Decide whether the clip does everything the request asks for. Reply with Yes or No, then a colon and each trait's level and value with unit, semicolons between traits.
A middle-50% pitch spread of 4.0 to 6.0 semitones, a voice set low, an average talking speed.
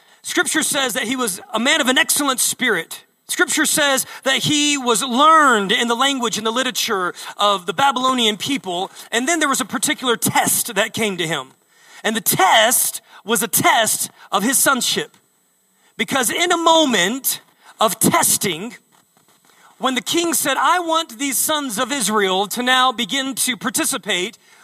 No: average, 4.5 semitones; very high, 260 Hz; average, 165 wpm